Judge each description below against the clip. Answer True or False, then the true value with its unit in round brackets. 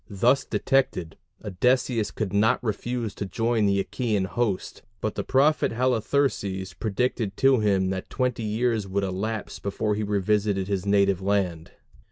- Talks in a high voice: False (105 Hz)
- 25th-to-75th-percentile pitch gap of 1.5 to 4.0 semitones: True (3.6 semitones)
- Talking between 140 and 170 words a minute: True (145 wpm)